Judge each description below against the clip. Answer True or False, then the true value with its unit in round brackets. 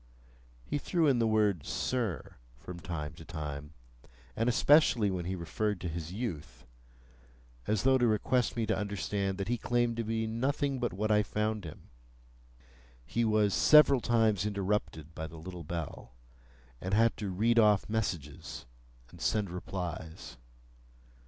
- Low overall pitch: True (100 Hz)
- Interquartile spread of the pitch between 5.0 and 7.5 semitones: True (5.6 semitones)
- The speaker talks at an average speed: True (150 wpm)